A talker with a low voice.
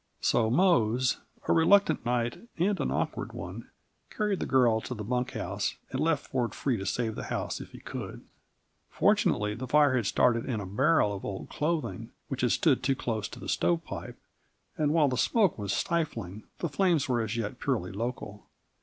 Yes: low, 125 Hz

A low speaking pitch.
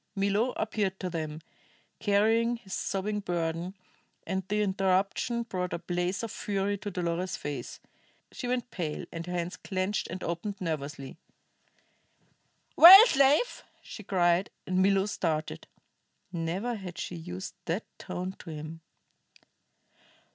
No: high, 190 Hz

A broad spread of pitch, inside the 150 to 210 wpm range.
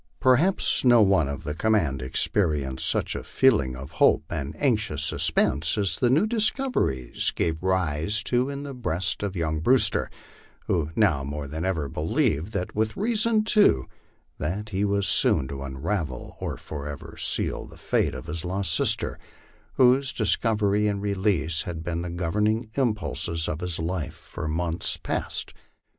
Yes: wide, 6.1 semitones; average, 160 wpm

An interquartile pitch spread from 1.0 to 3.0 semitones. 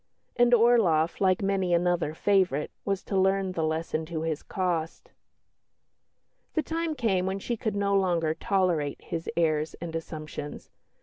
No: average, 3.6 semitones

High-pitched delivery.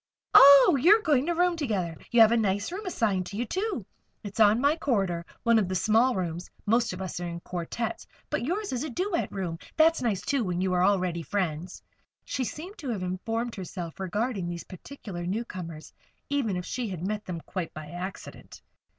Yes: high, 210 Hz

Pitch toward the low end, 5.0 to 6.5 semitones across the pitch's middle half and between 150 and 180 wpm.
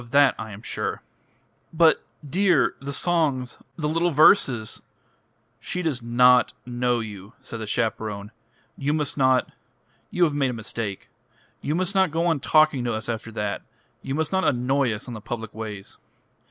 Yes: low, 125 Hz; average, 5.3 semitones; average, 175 wpm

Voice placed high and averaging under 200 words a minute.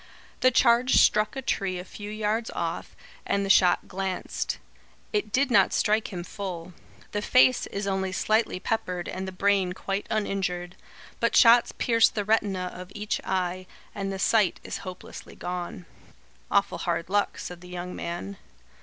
Yes: high, 195 Hz; average, 165 wpm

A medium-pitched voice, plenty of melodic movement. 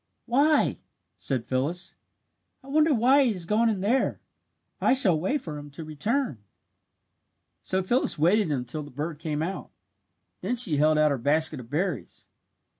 Yes: medium, 170 Hz; wide, 7.9 semitones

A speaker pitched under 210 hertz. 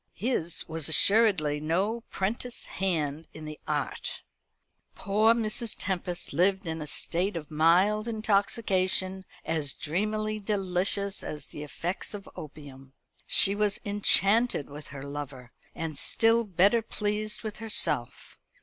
Yes: high, 190 Hz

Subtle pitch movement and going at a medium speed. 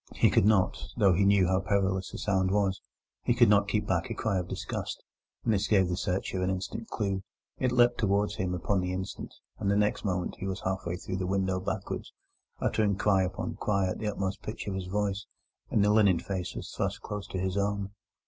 No: narrow, 1.8 semitones; fast, 220 wpm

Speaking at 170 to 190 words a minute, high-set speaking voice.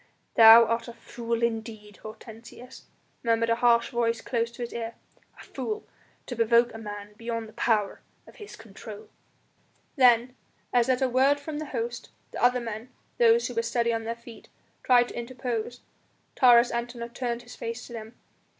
Yes: average, 175 wpm; high, 235 Hz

